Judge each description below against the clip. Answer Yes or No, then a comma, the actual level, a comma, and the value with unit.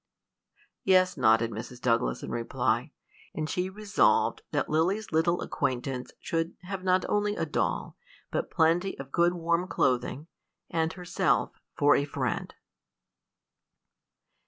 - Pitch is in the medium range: Yes, medium, 165 Hz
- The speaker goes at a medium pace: No, slow, 130 wpm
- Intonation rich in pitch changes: Yes, wide, 5.8 semitones